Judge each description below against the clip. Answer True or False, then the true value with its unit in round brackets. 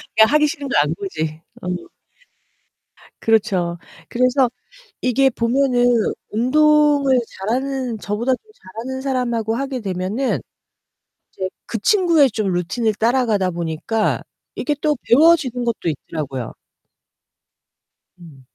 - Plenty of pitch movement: True (6.0 semitones)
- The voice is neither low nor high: False (235 Hz)